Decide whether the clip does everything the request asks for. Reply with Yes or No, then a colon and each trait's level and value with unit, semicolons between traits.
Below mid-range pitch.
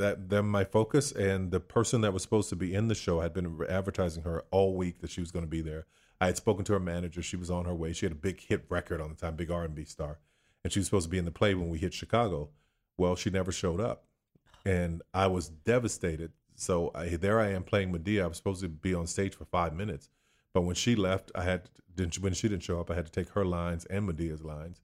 Yes: very low, 90 Hz